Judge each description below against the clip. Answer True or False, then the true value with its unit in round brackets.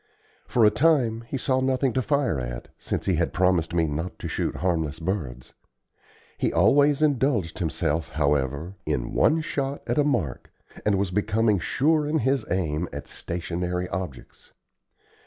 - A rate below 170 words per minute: True (155 wpm)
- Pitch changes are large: True (8.3 semitones)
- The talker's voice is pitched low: True (95 Hz)